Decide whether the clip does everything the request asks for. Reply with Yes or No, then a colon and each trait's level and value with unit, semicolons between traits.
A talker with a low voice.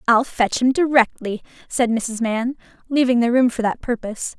No: high, 240 Hz